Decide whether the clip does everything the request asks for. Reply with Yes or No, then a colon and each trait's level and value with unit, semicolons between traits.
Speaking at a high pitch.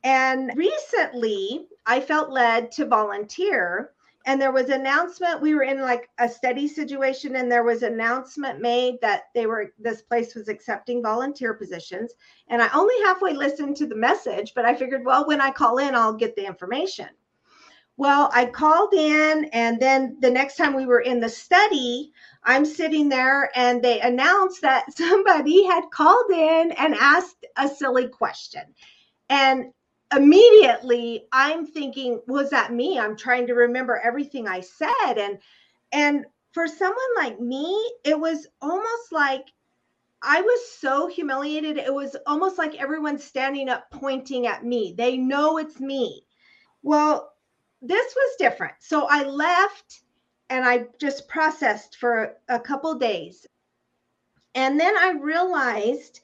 Yes: very high, 275 Hz